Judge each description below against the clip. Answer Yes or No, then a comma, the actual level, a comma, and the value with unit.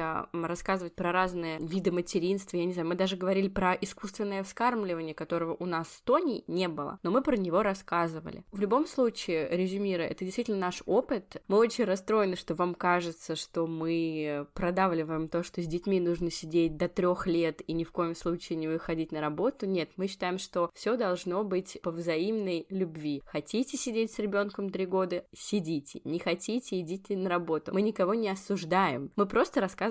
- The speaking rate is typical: No, fast, 180 wpm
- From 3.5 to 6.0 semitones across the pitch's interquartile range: No, average, 2.8 semitones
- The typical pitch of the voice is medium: Yes, medium, 180 Hz